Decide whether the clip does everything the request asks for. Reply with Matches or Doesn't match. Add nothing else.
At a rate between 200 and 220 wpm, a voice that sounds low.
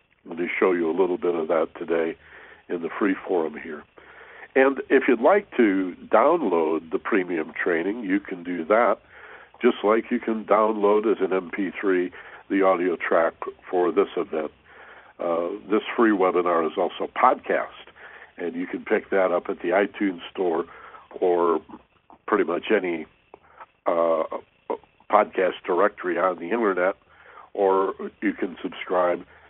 Doesn't match